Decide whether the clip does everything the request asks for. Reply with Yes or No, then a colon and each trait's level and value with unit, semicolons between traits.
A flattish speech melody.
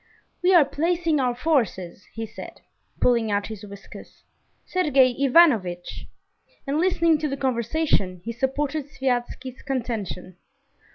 No: average, 5.3 semitones